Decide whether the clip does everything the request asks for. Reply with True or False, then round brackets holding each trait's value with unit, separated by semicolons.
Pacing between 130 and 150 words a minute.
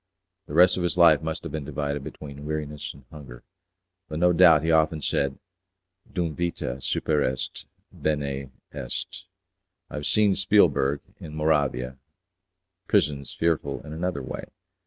True (145 wpm)